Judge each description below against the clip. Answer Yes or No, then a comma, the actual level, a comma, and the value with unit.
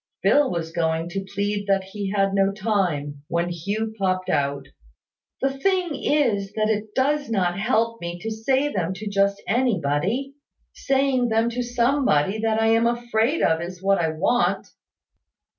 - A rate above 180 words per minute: No, average, 160 wpm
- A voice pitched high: Yes, high, 205 Hz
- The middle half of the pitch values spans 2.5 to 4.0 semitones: No, average, 4.6 semitones